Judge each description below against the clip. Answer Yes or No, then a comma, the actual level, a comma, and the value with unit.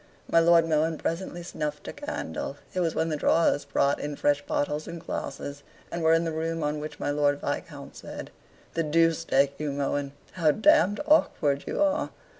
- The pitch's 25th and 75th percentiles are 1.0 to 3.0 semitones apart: Yes, narrow, 2.5 semitones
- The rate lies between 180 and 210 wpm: Yes, average, 190 wpm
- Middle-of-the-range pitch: Yes, medium, 155 Hz